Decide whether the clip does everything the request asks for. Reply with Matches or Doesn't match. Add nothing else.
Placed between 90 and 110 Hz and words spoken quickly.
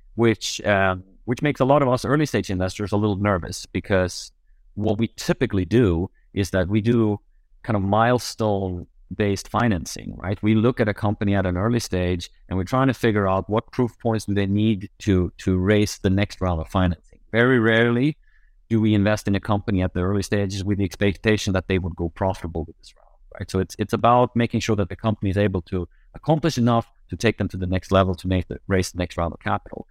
Matches